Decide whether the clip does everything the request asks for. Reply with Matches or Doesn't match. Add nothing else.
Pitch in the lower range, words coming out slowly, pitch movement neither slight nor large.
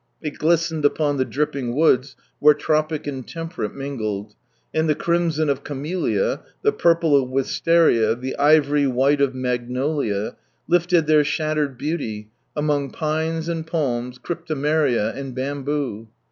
Doesn't match